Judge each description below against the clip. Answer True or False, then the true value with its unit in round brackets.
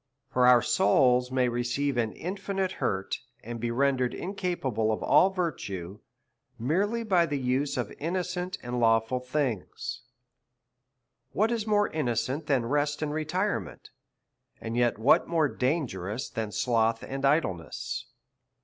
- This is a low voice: True (130 Hz)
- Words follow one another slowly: True (130 wpm)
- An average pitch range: False (6.0 semitones)